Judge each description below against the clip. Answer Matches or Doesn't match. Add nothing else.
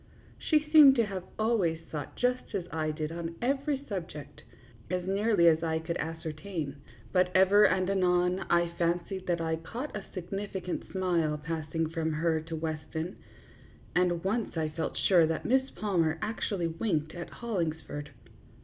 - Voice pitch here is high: Doesn't match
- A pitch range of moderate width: Matches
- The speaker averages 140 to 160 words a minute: Matches